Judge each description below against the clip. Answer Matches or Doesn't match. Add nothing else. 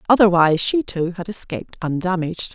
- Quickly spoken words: Doesn't match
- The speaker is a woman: Matches